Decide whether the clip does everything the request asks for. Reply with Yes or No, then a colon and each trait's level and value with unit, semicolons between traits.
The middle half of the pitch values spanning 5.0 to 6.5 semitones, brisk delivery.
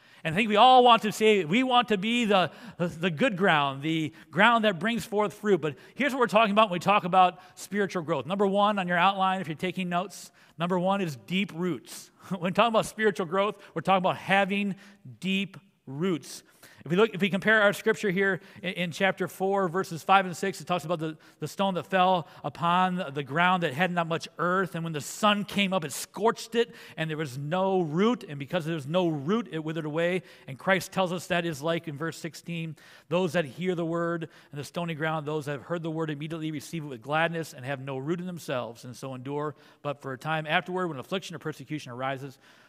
No: average, 3.5 semitones; fast, 230 wpm